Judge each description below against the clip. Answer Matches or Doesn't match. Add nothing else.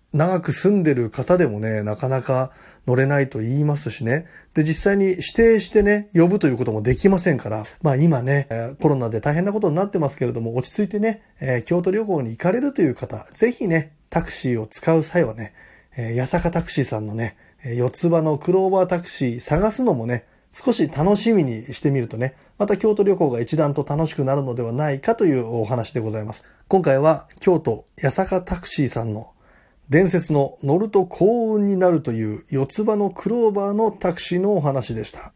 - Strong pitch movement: Matches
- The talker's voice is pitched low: Doesn't match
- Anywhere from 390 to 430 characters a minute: Doesn't match